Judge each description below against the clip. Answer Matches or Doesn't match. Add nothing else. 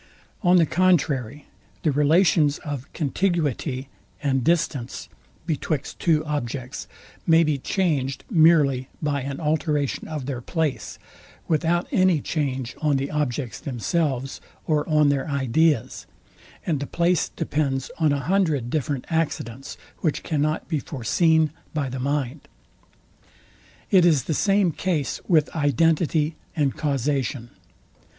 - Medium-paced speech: Doesn't match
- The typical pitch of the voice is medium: Matches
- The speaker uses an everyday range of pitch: Matches